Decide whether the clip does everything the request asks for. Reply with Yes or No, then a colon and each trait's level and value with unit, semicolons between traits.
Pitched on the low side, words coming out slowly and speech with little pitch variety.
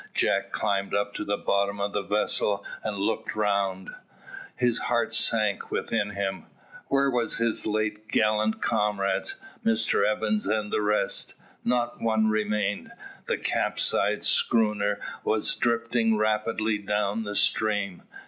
Yes: low, 105 Hz; slow, 130 wpm; narrow, 1.4 semitones